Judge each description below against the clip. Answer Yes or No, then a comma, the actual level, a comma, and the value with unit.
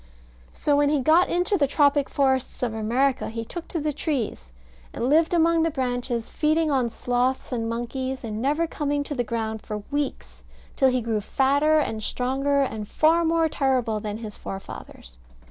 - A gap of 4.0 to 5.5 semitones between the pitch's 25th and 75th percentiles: Yes, average, 4.6 semitones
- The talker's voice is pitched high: Yes, very high, 265 Hz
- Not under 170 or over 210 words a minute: Yes, average, 180 wpm